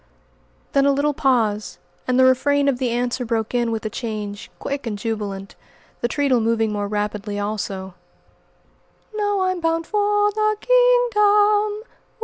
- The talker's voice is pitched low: No, very high, 255 Hz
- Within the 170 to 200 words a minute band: No, average, 145 wpm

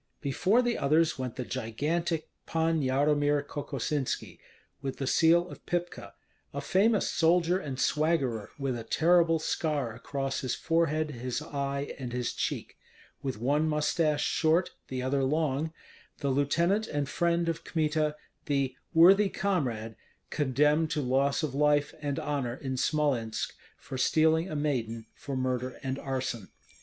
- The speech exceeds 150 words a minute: No, average, 145 wpm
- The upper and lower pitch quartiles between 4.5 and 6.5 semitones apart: No, average, 3.6 semitones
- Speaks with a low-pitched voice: No, medium, 145 Hz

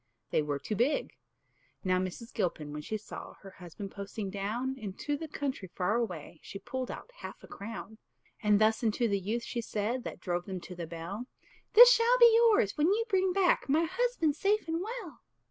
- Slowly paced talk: No, average, 195 wpm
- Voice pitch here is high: Yes, high, 225 Hz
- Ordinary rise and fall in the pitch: No, wide, 8.9 semitones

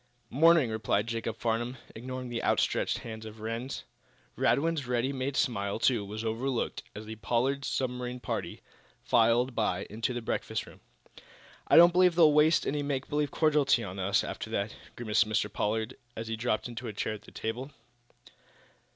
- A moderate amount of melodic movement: Yes, average, 3.4 semitones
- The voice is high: No, low, 120 Hz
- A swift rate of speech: No, average, 170 wpm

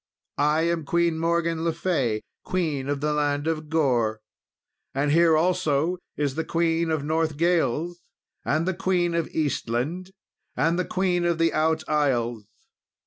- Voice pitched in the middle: Yes, medium, 160 Hz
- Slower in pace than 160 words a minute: Yes, average, 145 wpm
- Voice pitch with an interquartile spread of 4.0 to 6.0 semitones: No, average, 2.8 semitones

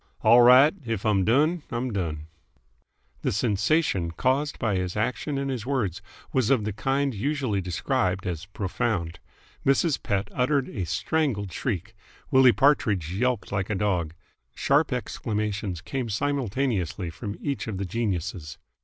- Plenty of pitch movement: Yes, wide, 5.8 semitones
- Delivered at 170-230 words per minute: No, average, 145 wpm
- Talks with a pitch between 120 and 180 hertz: No, low, 110 Hz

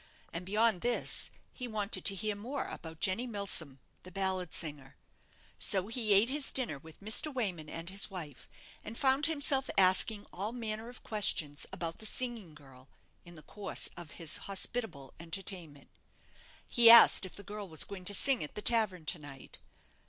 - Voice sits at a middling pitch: No, high, 195 Hz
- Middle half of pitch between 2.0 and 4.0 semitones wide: No, wide, 5.6 semitones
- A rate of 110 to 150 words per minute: No, average, 175 wpm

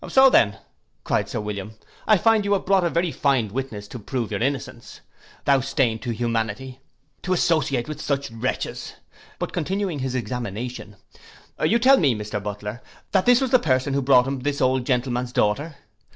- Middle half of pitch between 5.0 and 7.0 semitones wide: Yes, wide, 5.4 semitones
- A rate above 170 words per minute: Yes, average, 180 wpm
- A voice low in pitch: Yes, low, 130 Hz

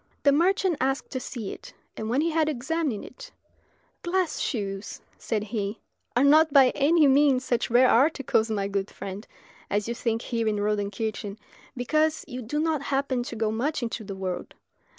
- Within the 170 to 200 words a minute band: Yes, average, 175 wpm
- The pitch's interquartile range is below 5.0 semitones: No, wide, 5.6 semitones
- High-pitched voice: Yes, high, 245 Hz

